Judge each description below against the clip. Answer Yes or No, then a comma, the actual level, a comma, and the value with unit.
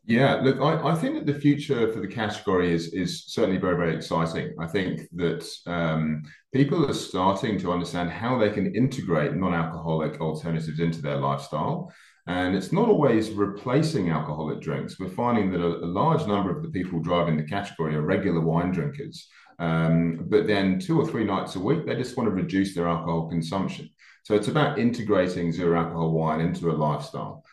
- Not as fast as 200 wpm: Yes, average, 185 wpm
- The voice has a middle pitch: No, very low, 85 Hz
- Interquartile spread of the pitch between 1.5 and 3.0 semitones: No, average, 4.0 semitones